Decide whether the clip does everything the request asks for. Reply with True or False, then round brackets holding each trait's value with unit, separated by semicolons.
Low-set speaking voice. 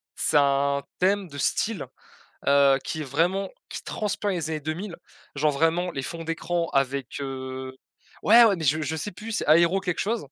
False (160 Hz)